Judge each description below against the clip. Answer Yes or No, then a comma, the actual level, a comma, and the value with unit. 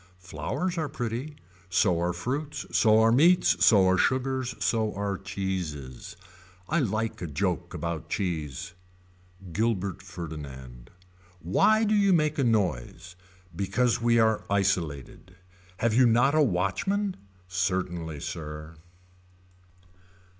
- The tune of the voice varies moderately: No, wide, 6.2 semitones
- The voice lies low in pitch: Yes, low, 100 Hz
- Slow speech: Yes, slow, 120 wpm